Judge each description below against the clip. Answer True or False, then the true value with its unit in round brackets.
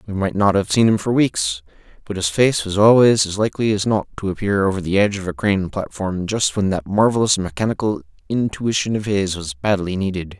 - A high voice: False (100 Hz)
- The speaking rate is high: True (215 wpm)